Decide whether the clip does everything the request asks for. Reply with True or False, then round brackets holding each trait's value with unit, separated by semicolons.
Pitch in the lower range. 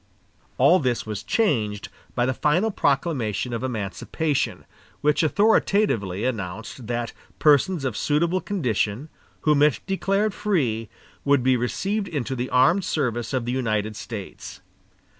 True (130 Hz)